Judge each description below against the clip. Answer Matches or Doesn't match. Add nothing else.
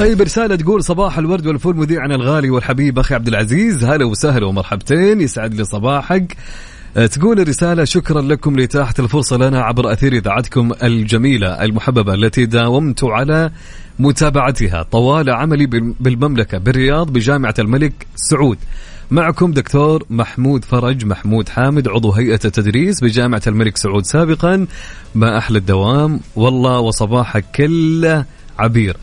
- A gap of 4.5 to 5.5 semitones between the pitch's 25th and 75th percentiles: Matches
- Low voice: Matches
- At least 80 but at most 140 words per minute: Matches